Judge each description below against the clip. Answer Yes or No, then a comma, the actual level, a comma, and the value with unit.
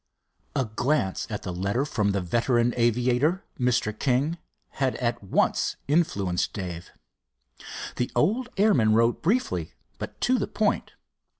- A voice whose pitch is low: Yes, low, 120 Hz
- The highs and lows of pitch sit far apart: Yes, wide, 6.2 semitones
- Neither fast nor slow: No, slow, 130 wpm